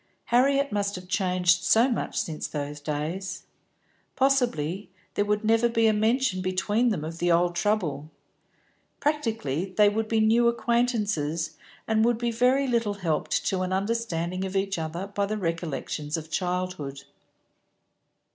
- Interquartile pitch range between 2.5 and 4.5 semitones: No, average, 4.9 semitones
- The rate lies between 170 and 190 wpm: No, average, 145 wpm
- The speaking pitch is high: Yes, high, 195 Hz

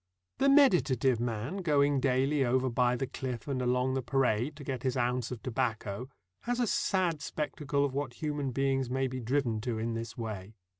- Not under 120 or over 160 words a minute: No, average, 190 wpm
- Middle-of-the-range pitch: No, low, 130 Hz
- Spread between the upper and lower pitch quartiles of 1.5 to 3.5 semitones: Yes, average, 2.9 semitones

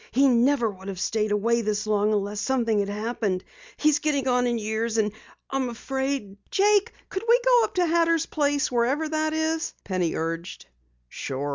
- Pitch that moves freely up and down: Yes, wide, 6.6 semitones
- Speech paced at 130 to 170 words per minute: No, average, 180 wpm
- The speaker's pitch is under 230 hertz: No, high, 240 Hz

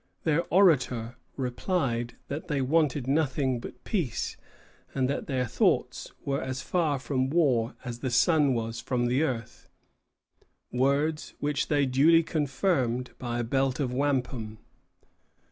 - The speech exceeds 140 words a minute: No, slow, 135 wpm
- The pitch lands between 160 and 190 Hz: No, low, 135 Hz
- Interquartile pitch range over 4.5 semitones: No, average, 3.3 semitones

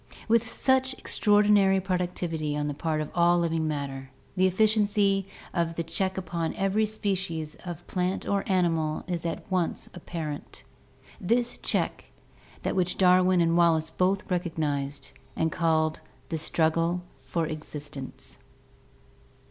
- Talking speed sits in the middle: No, slow, 130 wpm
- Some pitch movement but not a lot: Yes, average, 3.2 semitones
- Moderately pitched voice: Yes, medium, 175 Hz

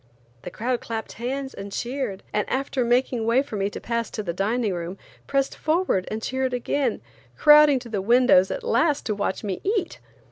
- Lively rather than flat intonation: No, average, 4.6 semitones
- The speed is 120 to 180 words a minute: No, average, 190 wpm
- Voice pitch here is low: No, high, 240 Hz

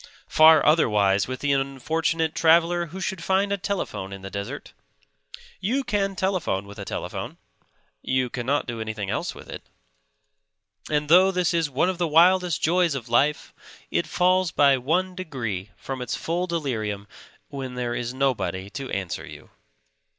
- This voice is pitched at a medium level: Yes, medium, 145 Hz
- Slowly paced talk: No, average, 160 wpm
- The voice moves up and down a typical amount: No, wide, 6.7 semitones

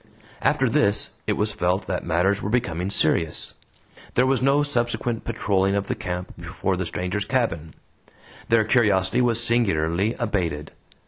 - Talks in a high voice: No, low, 100 Hz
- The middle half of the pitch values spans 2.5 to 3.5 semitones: No, average, 4.7 semitones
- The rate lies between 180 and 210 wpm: No, average, 145 wpm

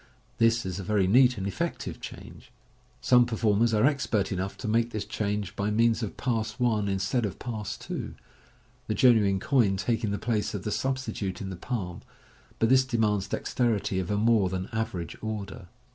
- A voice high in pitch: No, low, 105 Hz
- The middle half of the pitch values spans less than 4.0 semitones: Yes, average, 3.1 semitones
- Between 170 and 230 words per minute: Yes, average, 185 wpm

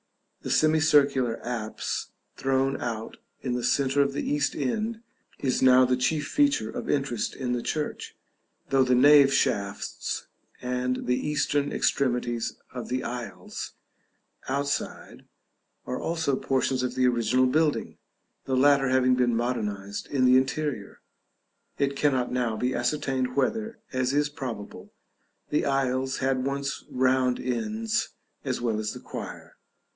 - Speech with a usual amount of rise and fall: No, narrow, 2.2 semitones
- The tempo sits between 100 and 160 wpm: Yes, average, 140 wpm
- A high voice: No, low, 130 Hz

